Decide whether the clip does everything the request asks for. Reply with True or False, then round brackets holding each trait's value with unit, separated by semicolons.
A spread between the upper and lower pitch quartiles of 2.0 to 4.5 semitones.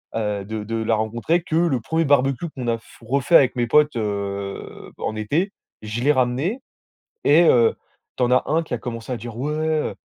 False (4.9 semitones)